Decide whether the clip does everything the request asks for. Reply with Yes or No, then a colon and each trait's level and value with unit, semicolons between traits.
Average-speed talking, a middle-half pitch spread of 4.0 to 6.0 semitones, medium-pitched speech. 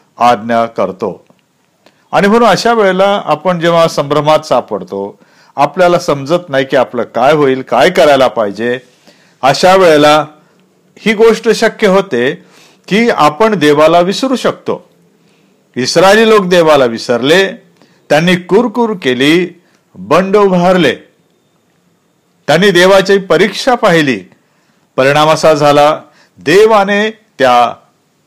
Yes: average, 105 wpm; wide, 5.6 semitones; medium, 175 Hz